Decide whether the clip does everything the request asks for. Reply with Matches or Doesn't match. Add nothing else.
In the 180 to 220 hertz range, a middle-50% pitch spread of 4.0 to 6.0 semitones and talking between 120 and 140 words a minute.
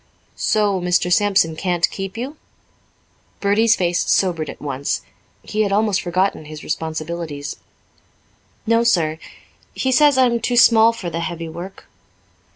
Matches